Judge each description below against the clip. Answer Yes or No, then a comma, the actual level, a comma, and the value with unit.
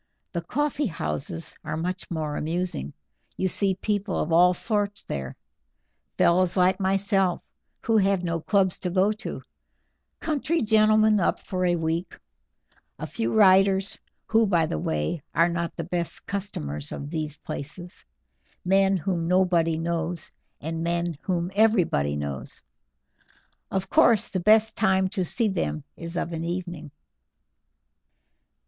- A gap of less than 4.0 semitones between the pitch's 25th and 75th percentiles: Yes, average, 3.1 semitones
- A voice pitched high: No, medium, 180 Hz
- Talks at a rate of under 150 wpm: Yes, average, 140 wpm